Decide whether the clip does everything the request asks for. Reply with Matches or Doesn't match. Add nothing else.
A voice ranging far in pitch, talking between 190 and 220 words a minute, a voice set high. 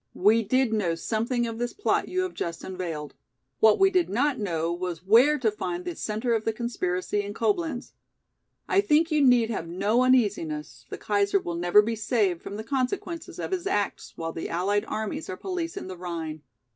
Matches